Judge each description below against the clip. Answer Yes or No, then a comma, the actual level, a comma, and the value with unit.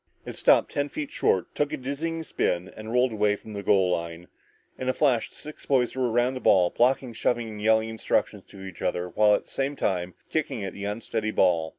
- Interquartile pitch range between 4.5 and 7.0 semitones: Yes, average, 5.1 semitones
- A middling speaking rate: No, fast, 225 wpm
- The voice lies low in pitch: Yes, low, 110 Hz